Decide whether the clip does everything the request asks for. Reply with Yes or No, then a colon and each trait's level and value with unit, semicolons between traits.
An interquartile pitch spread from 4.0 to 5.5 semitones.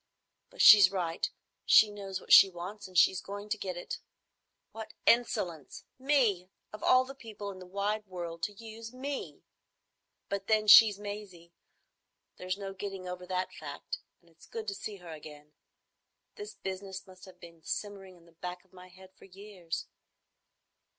No: average, 2.7 semitones